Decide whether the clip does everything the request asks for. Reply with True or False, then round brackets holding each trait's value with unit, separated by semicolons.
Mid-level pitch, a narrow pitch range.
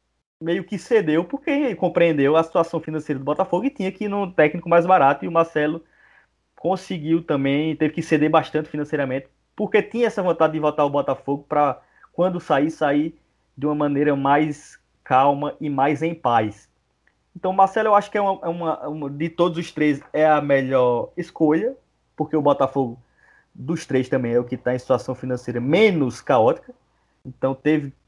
False (155 Hz; 3.6 semitones)